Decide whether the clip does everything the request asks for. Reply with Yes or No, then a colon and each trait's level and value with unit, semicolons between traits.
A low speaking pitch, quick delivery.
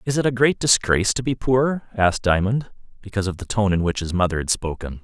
Yes: low, 105 Hz; fast, 240 wpm